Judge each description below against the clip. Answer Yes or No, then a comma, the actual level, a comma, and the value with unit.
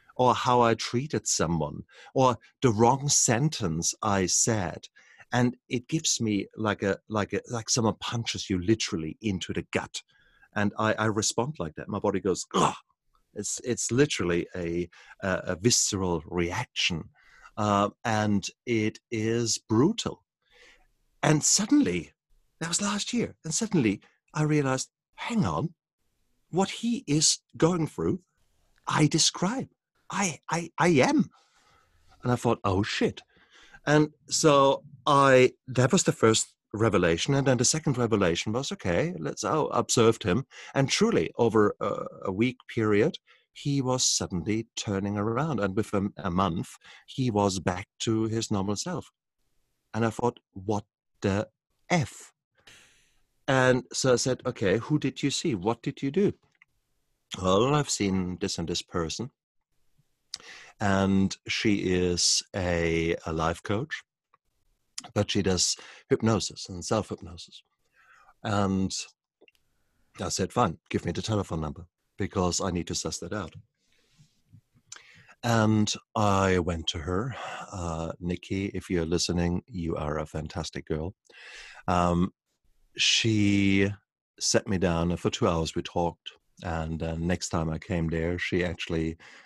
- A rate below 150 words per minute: Yes, average, 140 wpm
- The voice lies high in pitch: No, low, 105 Hz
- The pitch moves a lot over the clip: Yes, wide, 5.8 semitones